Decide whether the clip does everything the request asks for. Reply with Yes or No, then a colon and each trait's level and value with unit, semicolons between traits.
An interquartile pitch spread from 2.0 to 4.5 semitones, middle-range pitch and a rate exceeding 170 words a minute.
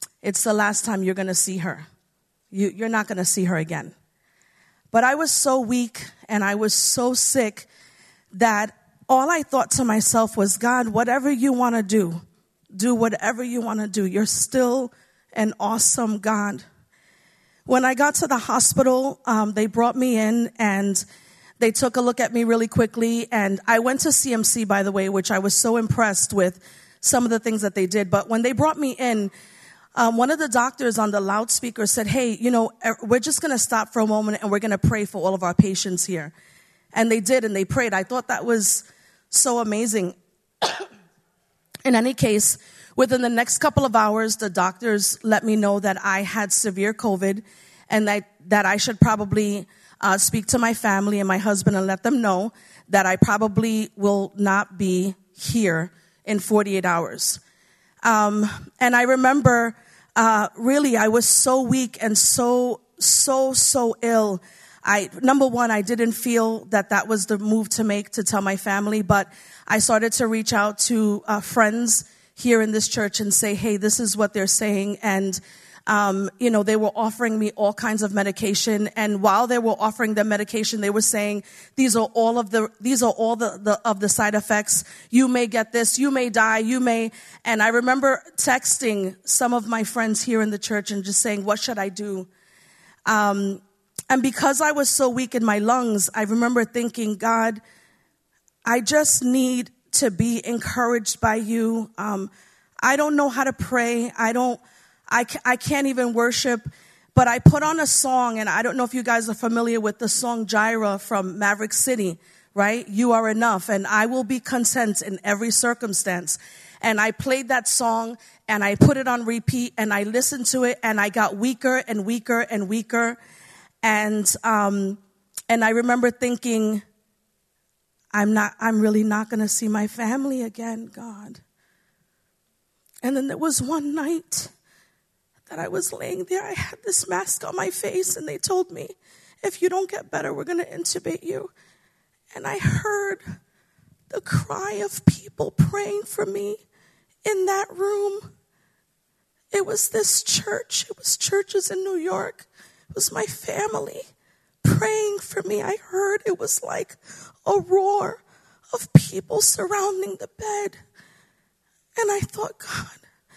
No: average, 3.3 semitones; high, 225 Hz; average, 180 wpm